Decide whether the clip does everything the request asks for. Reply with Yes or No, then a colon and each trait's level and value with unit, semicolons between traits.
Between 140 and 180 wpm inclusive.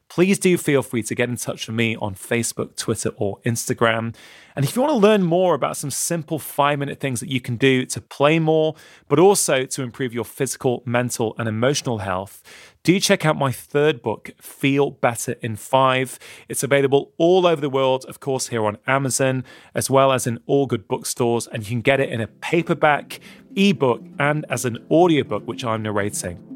No: average, 200 wpm